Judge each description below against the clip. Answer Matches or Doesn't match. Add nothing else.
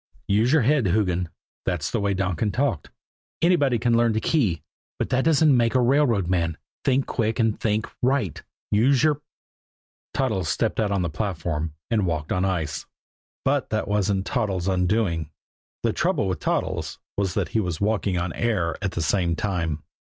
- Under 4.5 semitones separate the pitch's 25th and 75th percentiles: Doesn't match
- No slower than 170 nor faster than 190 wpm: Matches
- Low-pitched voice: Matches